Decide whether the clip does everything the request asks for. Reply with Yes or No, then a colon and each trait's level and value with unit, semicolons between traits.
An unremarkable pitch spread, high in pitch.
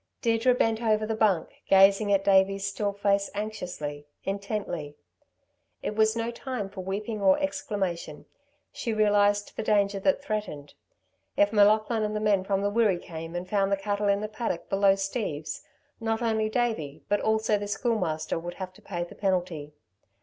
No: narrow, 2.3 semitones; high, 205 Hz